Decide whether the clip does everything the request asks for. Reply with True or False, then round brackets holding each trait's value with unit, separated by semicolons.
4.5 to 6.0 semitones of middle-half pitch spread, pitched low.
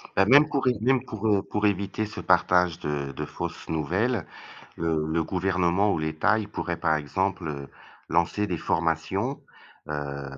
True (4.9 semitones; 90 Hz)